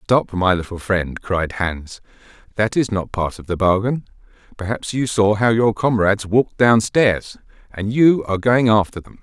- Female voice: No, male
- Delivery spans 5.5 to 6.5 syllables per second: No, 4.6 syllables/s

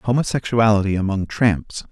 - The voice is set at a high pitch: No, low, 105 Hz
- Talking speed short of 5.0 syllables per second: Yes, 4.8 syllables/s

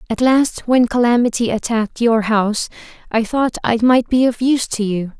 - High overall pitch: Yes, high, 235 Hz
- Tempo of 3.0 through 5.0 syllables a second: No, 5.2 syllables/s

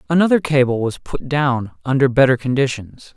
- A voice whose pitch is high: No, low, 135 Hz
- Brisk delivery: No, average, 150 wpm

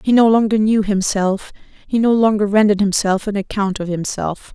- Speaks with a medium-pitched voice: No, high, 205 Hz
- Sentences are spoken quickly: No, average, 185 wpm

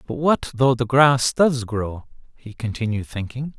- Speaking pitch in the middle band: No, low, 125 Hz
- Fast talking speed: No, average, 165 wpm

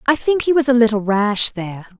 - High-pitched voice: Yes, high, 235 Hz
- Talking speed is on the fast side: Yes, fast, 240 wpm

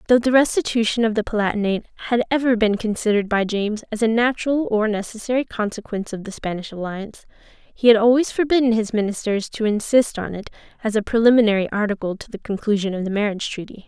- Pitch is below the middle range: No, high, 220 Hz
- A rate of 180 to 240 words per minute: Yes, average, 185 wpm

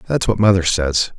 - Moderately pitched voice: No, very low, 90 Hz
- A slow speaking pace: No, fast, 205 wpm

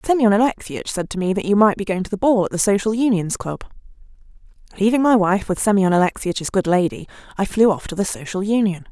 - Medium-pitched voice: No, high, 200 Hz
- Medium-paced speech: No, fast, 220 wpm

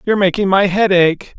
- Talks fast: Yes, fast, 215 wpm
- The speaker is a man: Yes, male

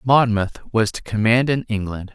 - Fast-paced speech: No, average, 170 wpm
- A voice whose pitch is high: No, low, 110 Hz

